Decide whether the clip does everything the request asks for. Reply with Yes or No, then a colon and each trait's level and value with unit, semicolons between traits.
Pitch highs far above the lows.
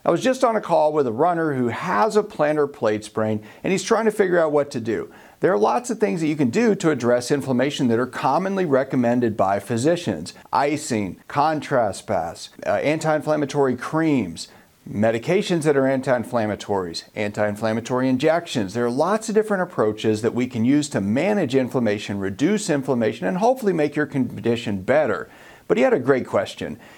Yes: wide, 6.8 semitones